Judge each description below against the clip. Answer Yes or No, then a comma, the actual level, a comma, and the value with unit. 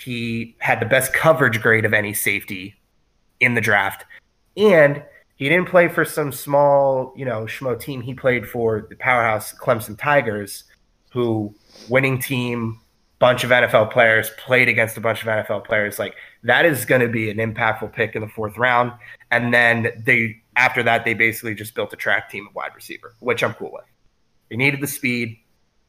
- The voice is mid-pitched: No, low, 120 Hz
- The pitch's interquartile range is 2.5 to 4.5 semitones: Yes, average, 2.9 semitones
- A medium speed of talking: Yes, average, 185 wpm